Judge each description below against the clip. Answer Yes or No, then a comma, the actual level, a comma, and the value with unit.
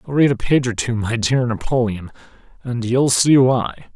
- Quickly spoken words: No, average, 180 wpm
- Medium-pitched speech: No, low, 120 Hz